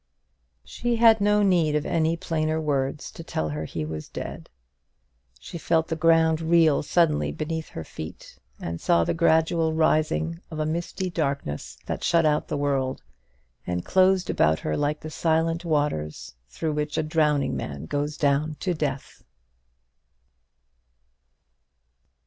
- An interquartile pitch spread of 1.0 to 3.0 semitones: Yes, average, 2.7 semitones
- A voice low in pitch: No, medium, 155 Hz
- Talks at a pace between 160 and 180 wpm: No, average, 145 wpm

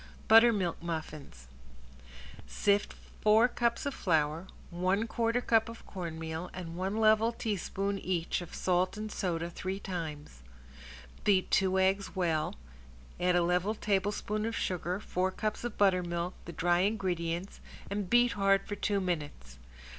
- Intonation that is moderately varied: Yes, average, 3.5 semitones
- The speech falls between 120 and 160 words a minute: Yes, average, 140 wpm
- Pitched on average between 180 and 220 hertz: Yes, medium, 185 Hz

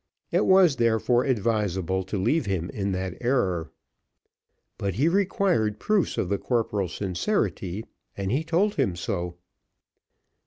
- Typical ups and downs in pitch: No, wide, 6.6 semitones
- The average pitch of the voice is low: Yes, low, 105 Hz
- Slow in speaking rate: Yes, slow, 130 wpm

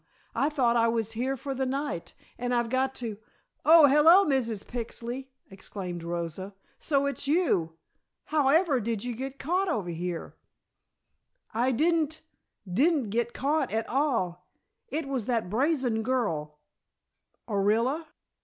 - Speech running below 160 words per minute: Yes, average, 140 wpm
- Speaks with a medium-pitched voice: No, high, 245 Hz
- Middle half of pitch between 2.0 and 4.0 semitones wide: No, average, 4.9 semitones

